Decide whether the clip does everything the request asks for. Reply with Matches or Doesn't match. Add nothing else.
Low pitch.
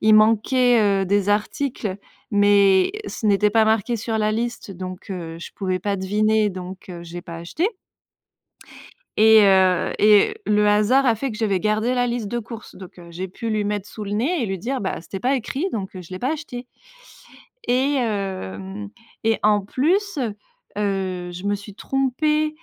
Doesn't match